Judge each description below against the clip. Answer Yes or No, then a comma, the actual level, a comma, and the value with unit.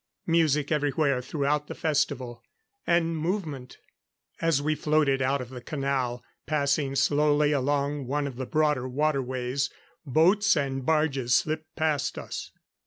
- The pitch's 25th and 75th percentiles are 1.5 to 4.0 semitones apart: Yes, narrow, 2.5 semitones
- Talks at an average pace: No, slow, 130 wpm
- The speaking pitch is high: No, medium, 145 Hz